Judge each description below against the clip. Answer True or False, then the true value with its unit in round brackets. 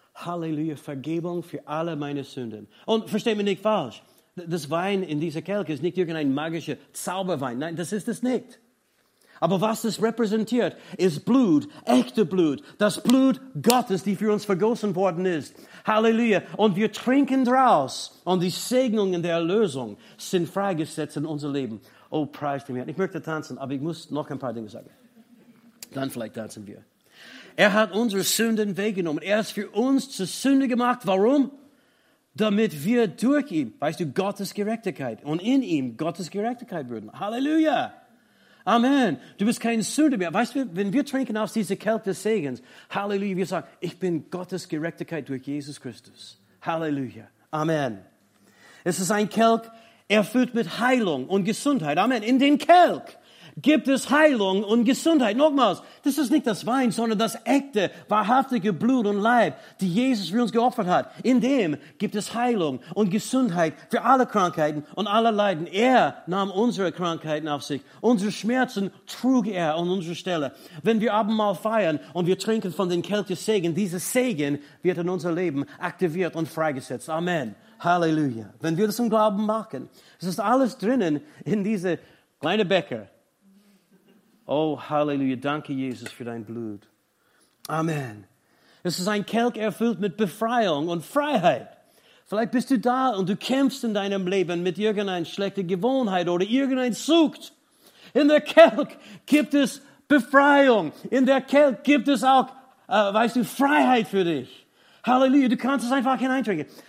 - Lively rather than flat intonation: True (6.4 semitones)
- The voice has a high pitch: True (205 Hz)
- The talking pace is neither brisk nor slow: True (165 wpm)